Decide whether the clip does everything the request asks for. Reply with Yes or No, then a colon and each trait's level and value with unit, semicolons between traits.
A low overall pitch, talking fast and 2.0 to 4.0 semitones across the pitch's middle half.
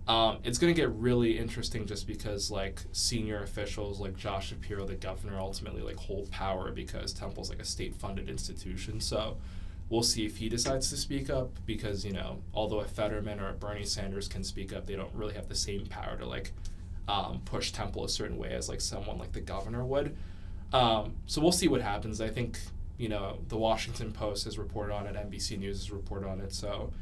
Yes: low, 100 Hz; fast, 210 wpm; narrow, 2.4 semitones